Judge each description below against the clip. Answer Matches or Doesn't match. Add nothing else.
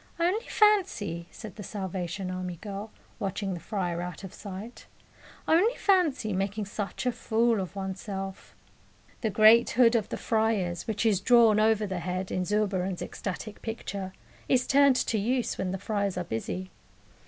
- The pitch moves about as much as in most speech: Matches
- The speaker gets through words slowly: Doesn't match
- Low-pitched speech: Doesn't match